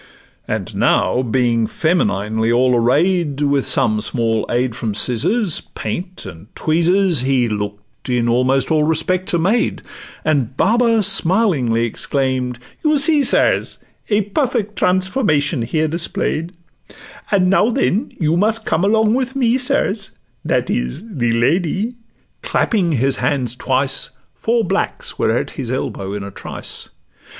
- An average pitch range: No, wide, 8.5 semitones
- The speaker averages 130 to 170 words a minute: Yes, slow, 135 wpm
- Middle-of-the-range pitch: Yes, medium, 155 Hz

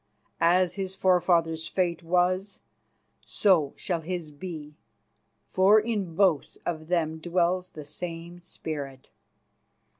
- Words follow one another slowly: Yes, slow, 110 wpm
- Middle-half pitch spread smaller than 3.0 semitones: Yes, narrow, 2.5 semitones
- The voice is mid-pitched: Yes, medium, 175 Hz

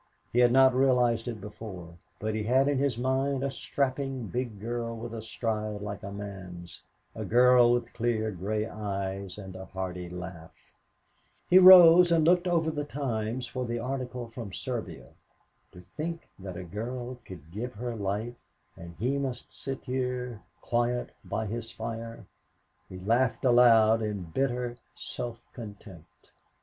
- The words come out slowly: No, average, 155 wpm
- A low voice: Yes, low, 115 Hz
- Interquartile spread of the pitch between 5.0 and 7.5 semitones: No, average, 3.8 semitones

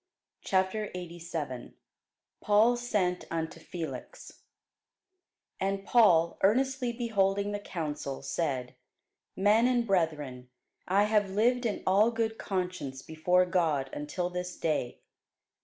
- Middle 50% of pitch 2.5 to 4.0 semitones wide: No, average, 4.7 semitones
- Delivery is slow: Yes, slow, 105 wpm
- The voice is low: No, medium, 185 Hz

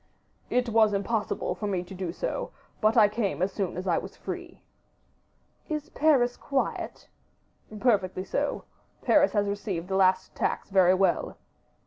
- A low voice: No, high, 200 Hz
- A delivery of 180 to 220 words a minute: No, average, 150 wpm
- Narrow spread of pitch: No, average, 3.7 semitones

